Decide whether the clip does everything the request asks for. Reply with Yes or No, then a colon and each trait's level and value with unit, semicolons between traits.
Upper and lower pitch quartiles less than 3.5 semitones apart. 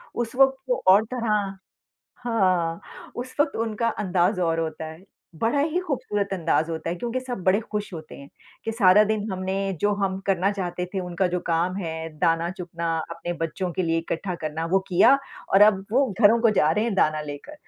No: average, 4.7 semitones